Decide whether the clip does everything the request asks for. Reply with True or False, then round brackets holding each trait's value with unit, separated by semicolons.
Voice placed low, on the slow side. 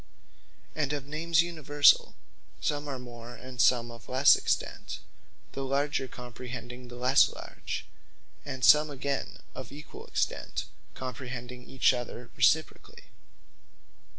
True (130 Hz; 125 wpm)